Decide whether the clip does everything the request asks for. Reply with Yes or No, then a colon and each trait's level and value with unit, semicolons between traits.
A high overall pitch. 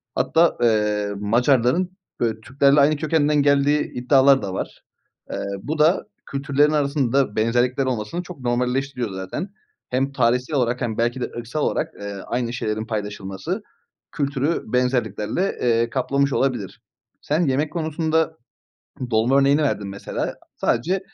No: low, 130 Hz